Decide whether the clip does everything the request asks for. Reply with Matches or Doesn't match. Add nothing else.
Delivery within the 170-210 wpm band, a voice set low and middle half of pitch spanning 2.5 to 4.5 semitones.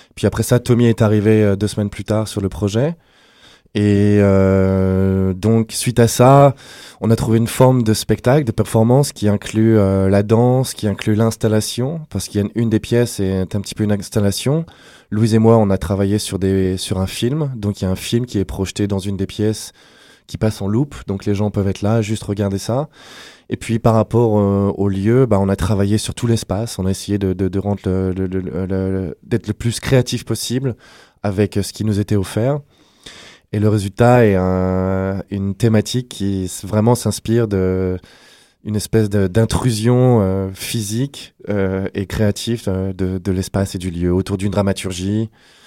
Matches